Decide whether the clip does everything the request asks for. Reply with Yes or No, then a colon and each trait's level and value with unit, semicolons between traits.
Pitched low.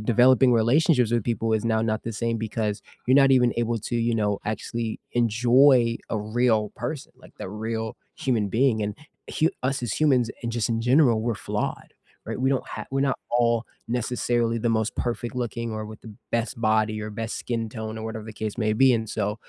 Yes: low, 115 Hz